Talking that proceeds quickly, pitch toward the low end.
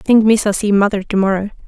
No: fast, 215 wpm; high, 205 Hz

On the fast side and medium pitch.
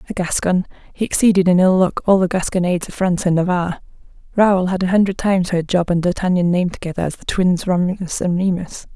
Yes: fast, 210 wpm; medium, 180 Hz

